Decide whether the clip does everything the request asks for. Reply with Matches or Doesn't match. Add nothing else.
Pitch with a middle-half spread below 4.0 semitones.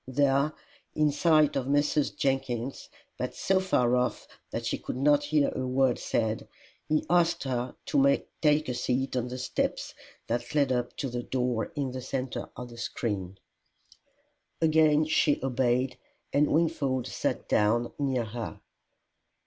Matches